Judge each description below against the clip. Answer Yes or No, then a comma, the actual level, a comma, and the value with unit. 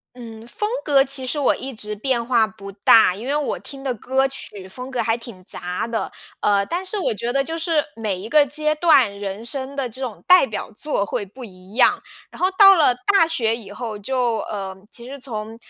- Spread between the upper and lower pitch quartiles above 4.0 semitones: Yes, average, 4.6 semitones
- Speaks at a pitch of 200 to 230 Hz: No, high, 240 Hz